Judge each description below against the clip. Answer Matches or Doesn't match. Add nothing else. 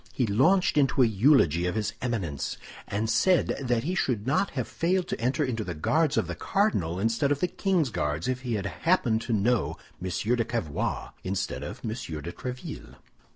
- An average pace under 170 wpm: Doesn't match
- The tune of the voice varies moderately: Doesn't match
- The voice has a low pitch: Matches